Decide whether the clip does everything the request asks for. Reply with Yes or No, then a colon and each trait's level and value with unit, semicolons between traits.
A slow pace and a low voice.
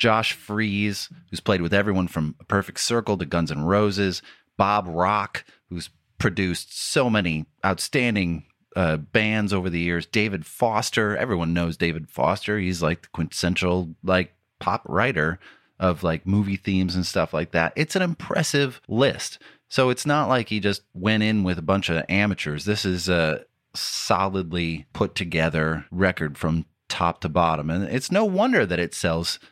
No: average, 160 wpm; very low, 95 Hz